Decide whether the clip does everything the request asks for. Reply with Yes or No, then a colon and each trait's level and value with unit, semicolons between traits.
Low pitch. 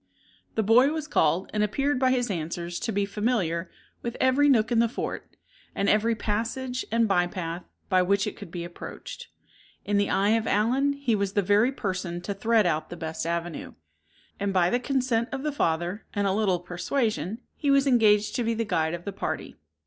No: high, 210 Hz